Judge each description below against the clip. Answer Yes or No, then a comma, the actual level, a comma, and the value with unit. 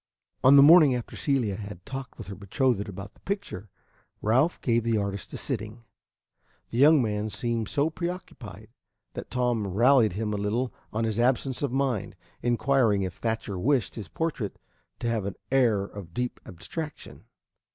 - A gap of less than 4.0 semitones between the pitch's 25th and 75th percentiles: No, average, 4.5 semitones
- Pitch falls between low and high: No, low, 115 Hz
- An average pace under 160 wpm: No, average, 165 wpm